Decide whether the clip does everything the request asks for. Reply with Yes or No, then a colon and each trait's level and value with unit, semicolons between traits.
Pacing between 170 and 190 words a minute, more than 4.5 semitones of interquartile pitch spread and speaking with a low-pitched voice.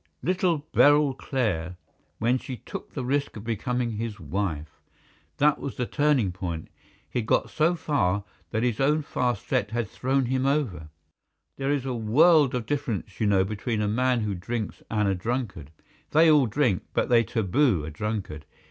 Yes: average, 175 wpm; average, 5.3 semitones; low, 120 Hz